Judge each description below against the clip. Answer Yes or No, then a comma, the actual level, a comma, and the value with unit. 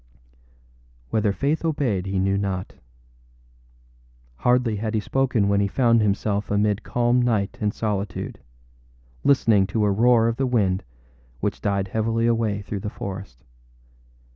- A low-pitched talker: Yes, low, 105 Hz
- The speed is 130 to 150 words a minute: Yes, average, 140 wpm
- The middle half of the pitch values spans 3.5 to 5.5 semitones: No, average, 2.9 semitones